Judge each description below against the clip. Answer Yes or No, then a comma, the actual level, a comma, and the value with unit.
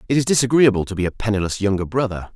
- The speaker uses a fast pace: Yes, fast, 230 wpm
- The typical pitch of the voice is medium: No, low, 110 Hz